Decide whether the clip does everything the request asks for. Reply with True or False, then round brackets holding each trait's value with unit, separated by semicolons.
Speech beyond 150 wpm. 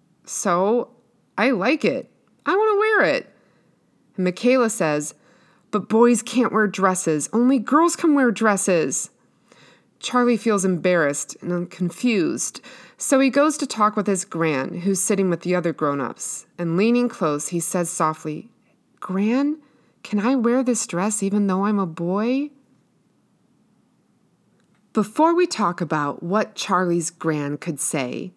False (140 wpm)